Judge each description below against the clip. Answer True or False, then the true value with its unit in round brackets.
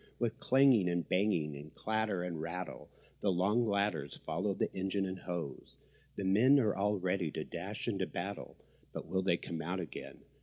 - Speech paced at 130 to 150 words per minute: False (180 wpm)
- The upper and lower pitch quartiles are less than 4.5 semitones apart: True (3.2 semitones)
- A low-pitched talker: True (95 Hz)